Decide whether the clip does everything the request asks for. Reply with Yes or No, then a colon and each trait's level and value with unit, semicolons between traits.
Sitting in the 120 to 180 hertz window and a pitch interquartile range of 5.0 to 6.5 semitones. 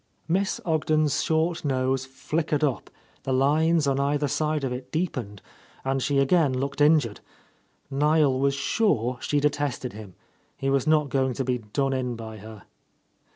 No: medium, 140 Hz; average, 3.0 semitones